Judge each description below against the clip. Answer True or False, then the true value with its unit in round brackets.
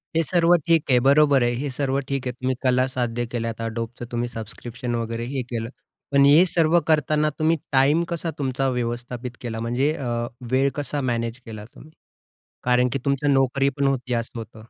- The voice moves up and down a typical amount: True (3.1 semitones)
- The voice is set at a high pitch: False (130 Hz)